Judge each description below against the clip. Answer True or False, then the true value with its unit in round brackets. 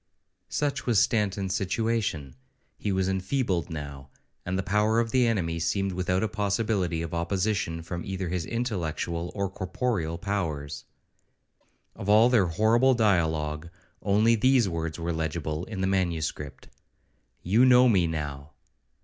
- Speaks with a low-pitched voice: True (95 Hz)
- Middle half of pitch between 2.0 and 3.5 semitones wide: False (4.7 semitones)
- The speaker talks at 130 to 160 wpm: True (140 wpm)